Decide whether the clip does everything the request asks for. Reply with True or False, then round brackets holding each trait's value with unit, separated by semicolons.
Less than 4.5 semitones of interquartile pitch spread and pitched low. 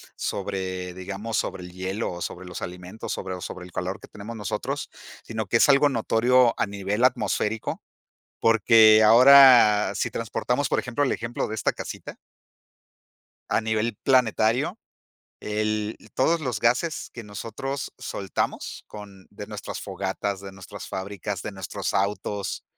True (3.3 semitones; 105 Hz)